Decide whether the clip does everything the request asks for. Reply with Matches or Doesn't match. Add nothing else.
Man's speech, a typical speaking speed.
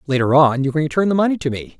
Doesn't match